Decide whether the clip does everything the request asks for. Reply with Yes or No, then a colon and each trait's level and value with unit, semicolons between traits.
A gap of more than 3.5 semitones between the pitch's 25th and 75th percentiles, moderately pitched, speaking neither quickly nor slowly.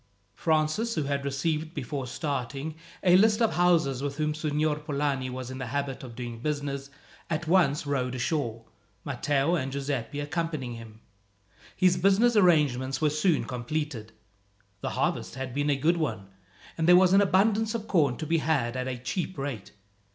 Yes: average, 4.1 semitones; medium, 145 Hz; average, 170 wpm